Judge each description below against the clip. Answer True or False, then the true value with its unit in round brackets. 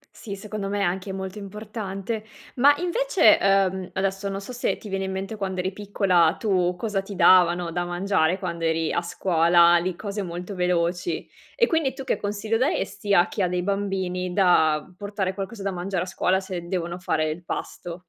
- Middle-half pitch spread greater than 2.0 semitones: True (2.4 semitones)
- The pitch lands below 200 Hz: True (190 Hz)